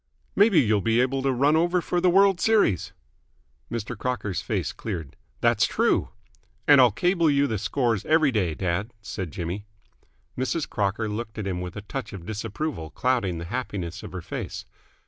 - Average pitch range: No, wide, 6.6 semitones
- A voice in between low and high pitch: No, low, 115 Hz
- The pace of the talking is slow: No, average, 175 wpm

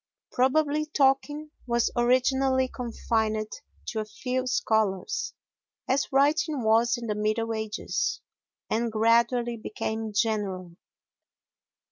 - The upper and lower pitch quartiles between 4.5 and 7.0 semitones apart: No, average, 3.4 semitones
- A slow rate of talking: Yes, slow, 100 wpm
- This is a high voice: Yes, high, 235 Hz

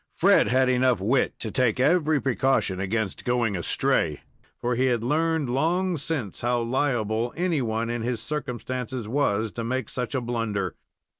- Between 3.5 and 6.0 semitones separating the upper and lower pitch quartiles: No, average, 3.0 semitones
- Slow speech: No, average, 160 wpm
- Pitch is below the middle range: Yes, low, 125 Hz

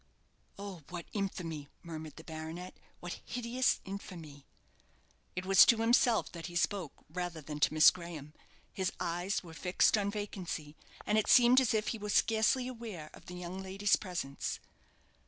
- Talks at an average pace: Yes, average, 160 wpm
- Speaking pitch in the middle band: Yes, medium, 180 Hz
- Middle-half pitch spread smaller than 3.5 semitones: No, average, 4.2 semitones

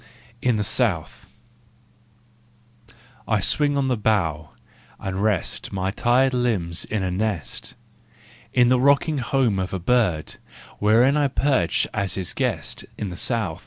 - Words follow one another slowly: No, average, 145 wpm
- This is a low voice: Yes, low, 110 Hz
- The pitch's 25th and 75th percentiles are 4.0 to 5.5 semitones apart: Yes, average, 5.2 semitones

